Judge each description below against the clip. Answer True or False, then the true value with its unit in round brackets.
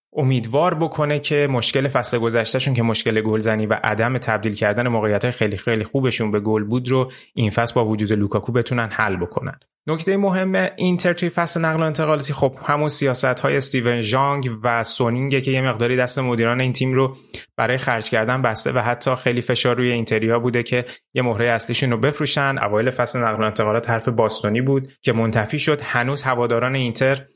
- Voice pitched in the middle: False (125 Hz)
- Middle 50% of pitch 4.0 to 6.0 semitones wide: False (3.0 semitones)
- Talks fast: True (185 wpm)